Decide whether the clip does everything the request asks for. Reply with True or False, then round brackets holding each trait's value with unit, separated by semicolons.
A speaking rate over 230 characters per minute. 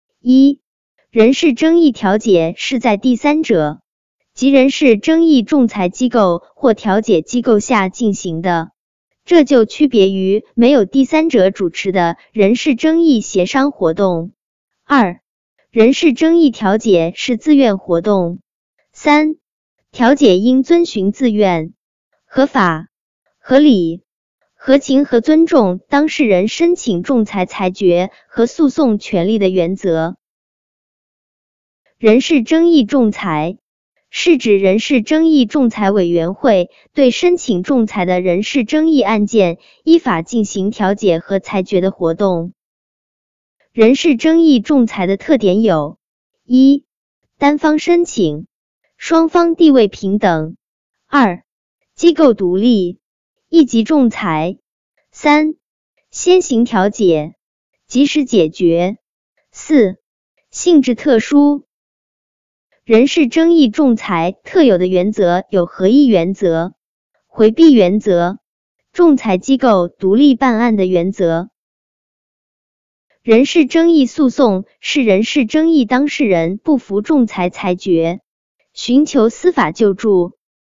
False (180 characters per minute)